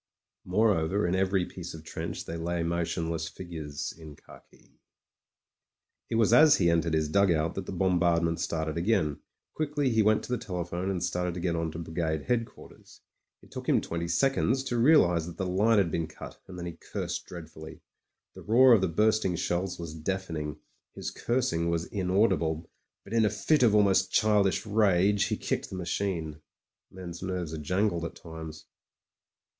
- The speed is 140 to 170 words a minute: No, average, 185 wpm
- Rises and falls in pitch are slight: No, average, 3.7 semitones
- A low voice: Yes, very low, 90 Hz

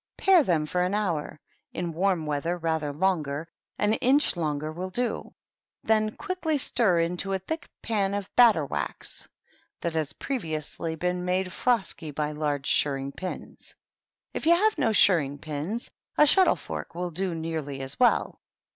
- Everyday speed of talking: Yes, average, 160 wpm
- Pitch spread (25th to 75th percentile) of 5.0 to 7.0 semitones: Yes, wide, 5.6 semitones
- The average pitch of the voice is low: No, medium, 180 Hz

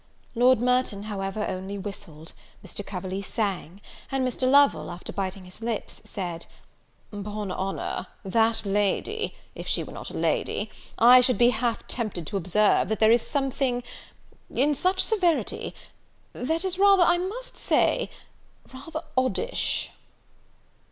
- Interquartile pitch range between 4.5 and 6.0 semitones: Yes, wide, 5.5 semitones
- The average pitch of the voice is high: Yes, high, 225 Hz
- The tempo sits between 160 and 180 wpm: No, average, 140 wpm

